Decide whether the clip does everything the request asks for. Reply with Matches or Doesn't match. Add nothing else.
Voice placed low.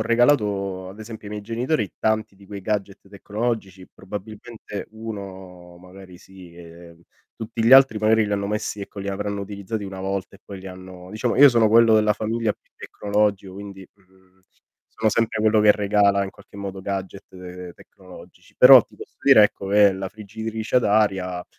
Matches